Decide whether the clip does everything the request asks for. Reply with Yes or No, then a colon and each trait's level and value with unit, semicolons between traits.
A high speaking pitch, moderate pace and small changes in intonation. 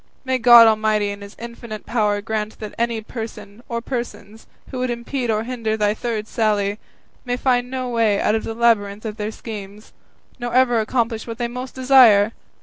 Yes: high, 225 Hz; average, 185 wpm; narrow, 2.3 semitones